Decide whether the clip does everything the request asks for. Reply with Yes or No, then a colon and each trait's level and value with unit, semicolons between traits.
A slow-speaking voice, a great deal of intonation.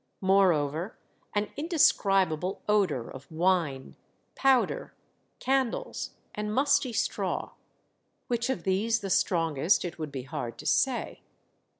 Yes: slow, 110 wpm; wide, 6.4 semitones